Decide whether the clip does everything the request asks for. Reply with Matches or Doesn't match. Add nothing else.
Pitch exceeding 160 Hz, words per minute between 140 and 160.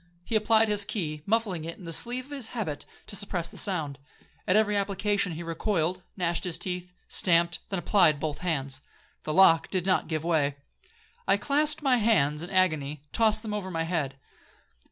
Doesn't match